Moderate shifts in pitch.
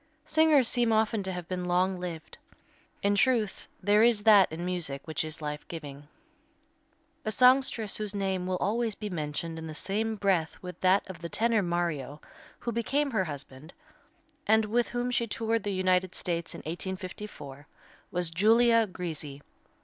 Yes: average, 4.8 semitones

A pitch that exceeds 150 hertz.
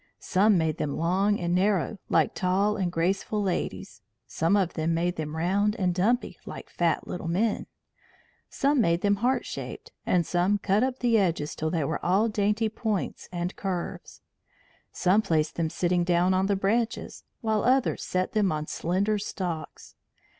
Yes: high, 190 Hz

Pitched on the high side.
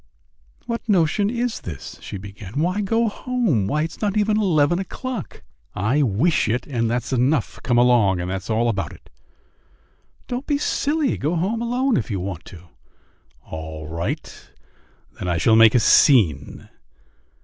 No: low, 130 Hz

